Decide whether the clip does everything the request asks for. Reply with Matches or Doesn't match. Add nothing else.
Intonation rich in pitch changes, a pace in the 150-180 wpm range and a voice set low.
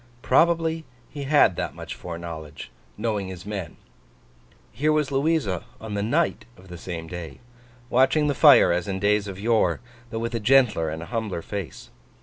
Matches